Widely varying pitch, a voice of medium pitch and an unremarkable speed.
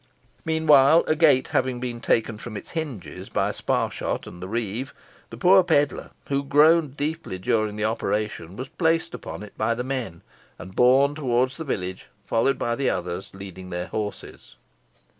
No: wide, 5.8 semitones; low, 125 Hz; average, 165 wpm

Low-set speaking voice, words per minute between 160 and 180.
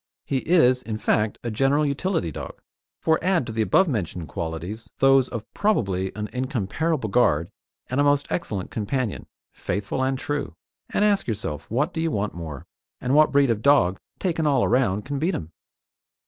Yes: low, 125 Hz; average, 175 wpm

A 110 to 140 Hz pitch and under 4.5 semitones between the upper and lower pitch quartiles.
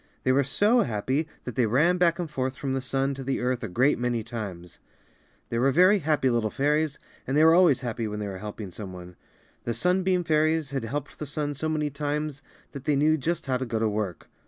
No: low, 135 Hz; average, 4.8 semitones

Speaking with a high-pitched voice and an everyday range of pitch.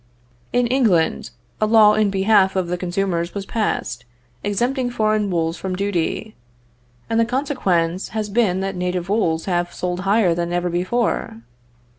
Yes: high, 195 Hz; average, 3.7 semitones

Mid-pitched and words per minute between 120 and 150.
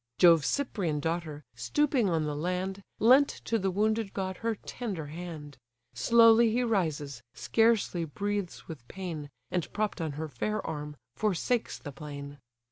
Yes: medium, 180 Hz; average, 145 wpm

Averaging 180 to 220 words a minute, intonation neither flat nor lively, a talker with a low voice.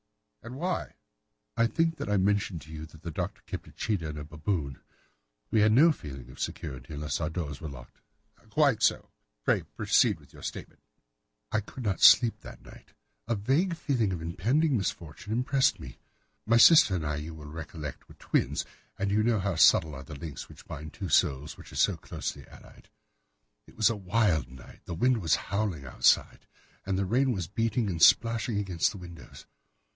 No: average, 190 wpm; wide, 6.8 semitones; very low, 95 Hz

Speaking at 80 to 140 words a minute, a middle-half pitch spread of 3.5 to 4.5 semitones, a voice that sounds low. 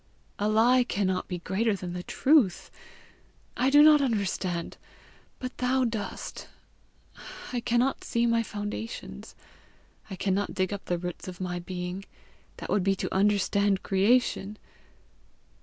No: slow, 135 wpm; average, 4.1 semitones; high, 205 Hz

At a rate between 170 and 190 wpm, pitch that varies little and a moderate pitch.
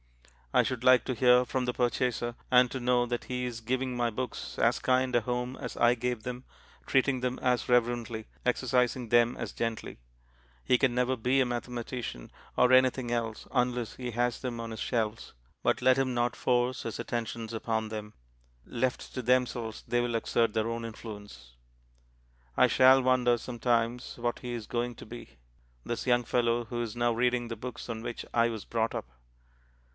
No: average, 185 wpm; narrow, 1.4 semitones; low, 120 Hz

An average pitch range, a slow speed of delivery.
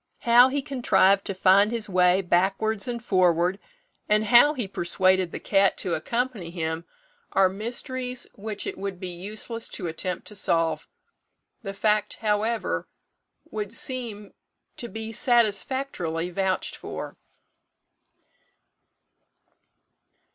Yes: average, 3.9 semitones; slow, 120 wpm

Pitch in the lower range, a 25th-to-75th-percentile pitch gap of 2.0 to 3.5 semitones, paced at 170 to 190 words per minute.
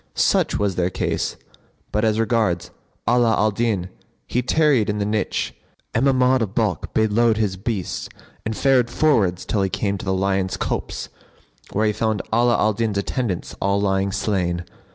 Yes: low, 105 Hz; average, 3.2 semitones; average, 175 wpm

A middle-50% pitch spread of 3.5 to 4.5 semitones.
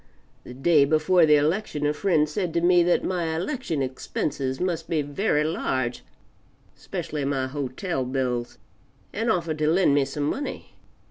Yes: average, 4.0 semitones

